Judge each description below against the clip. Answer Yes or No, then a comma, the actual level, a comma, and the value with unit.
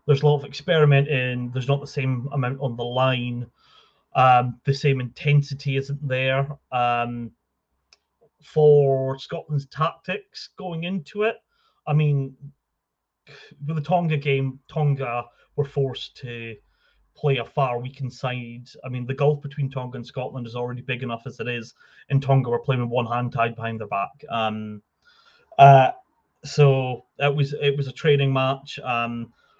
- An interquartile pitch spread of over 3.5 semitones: No, average, 2.9 semitones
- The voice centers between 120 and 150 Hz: Yes, low, 135 Hz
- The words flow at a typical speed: Yes, average, 160 wpm